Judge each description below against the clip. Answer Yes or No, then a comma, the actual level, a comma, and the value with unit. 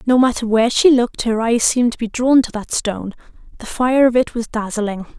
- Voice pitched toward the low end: No, high, 235 Hz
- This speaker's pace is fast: Yes, fast, 230 wpm